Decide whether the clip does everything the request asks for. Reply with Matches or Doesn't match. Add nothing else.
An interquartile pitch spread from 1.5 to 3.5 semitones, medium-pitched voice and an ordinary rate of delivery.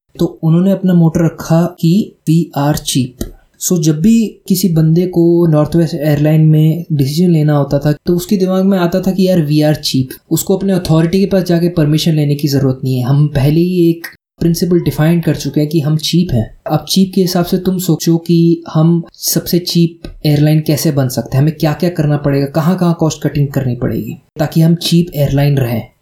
Doesn't match